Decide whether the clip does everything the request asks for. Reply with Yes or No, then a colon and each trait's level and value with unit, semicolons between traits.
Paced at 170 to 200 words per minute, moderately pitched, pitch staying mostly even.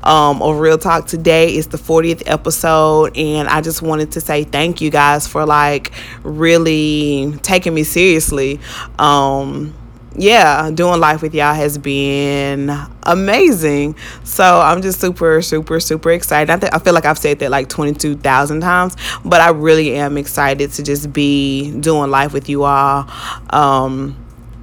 No: average, 155 wpm; medium, 150 Hz; narrow, 2.3 semitones